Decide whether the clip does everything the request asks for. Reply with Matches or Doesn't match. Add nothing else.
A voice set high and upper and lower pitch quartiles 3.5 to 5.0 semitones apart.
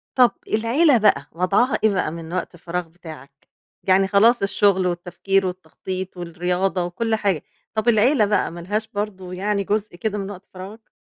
Doesn't match